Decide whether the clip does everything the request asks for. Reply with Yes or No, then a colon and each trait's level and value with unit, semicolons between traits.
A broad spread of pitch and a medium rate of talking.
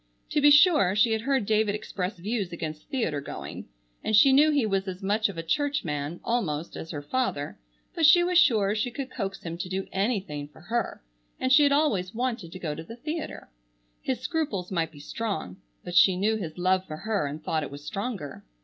No: wide, 7.1 semitones; fast, 215 wpm